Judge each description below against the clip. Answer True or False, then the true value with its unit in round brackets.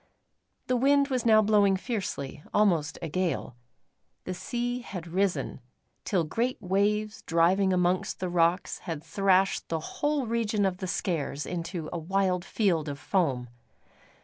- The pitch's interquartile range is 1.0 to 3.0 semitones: False (4.1 semitones)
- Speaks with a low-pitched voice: False (185 Hz)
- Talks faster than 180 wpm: False (145 wpm)